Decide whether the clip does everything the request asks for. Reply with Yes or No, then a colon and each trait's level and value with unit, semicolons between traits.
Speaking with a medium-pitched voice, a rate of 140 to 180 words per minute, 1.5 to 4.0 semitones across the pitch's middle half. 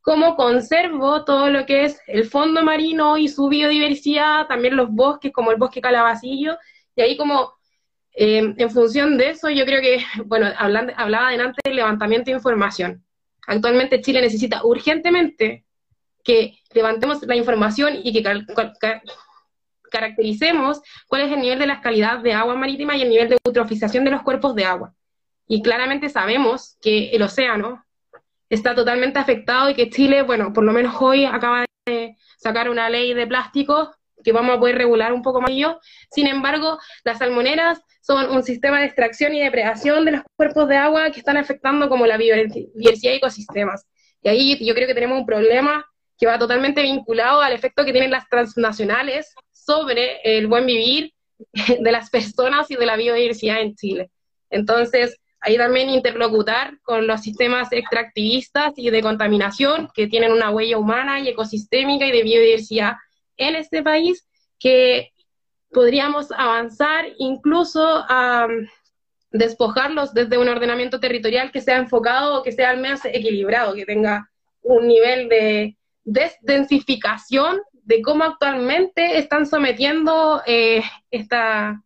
No: very high, 250 Hz; average, 160 wpm; average, 3.7 semitones